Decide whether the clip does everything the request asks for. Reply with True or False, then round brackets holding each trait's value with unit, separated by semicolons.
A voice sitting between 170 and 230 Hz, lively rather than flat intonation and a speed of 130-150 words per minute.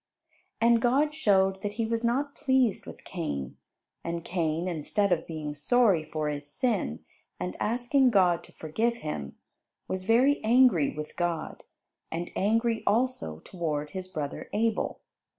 True (190 Hz; 6.9 semitones; 145 wpm)